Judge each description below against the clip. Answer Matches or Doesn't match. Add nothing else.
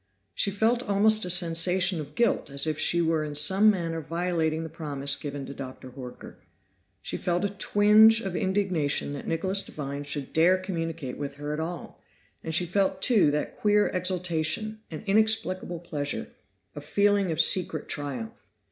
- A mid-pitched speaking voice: Matches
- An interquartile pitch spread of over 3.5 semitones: Matches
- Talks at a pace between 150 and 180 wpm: Matches